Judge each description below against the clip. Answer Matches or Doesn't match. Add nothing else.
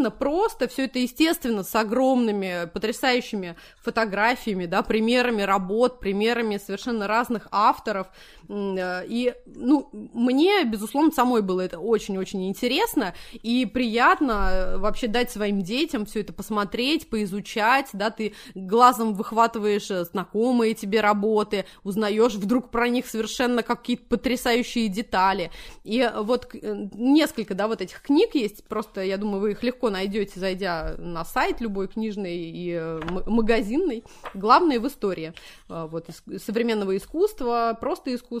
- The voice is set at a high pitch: Matches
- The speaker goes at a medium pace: Matches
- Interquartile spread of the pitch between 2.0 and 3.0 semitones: Doesn't match